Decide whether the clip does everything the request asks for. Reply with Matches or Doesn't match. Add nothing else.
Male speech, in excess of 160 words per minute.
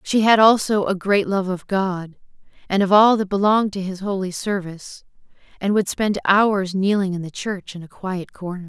Doesn't match